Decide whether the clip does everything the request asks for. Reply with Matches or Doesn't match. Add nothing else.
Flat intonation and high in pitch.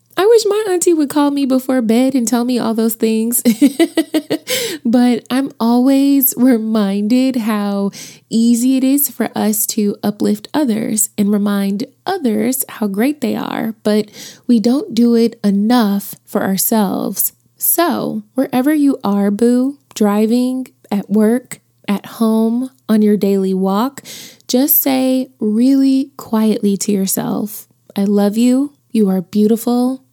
Doesn't match